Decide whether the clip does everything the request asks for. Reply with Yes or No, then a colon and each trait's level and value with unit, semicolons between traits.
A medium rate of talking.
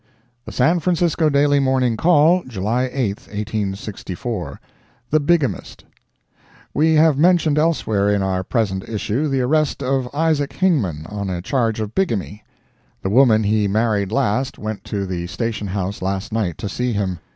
Yes: average, 150 wpm